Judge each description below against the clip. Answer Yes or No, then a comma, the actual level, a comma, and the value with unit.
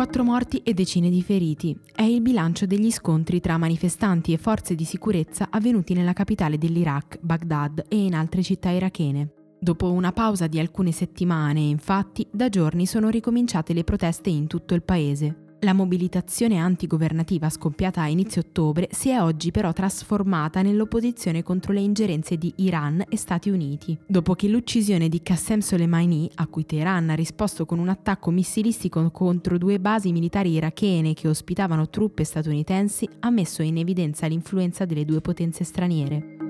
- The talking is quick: No, average, 160 wpm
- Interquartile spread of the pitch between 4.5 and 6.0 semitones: No, average, 3.4 semitones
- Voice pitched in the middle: Yes, medium, 180 Hz